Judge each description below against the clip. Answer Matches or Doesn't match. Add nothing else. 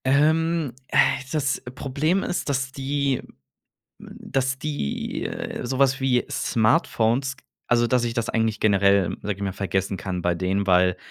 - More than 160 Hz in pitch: Doesn't match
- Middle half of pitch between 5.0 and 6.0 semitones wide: Matches